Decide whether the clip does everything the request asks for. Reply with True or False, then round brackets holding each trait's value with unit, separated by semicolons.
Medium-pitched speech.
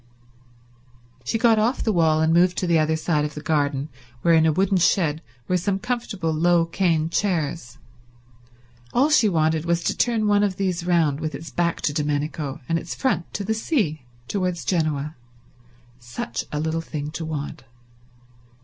True (165 Hz)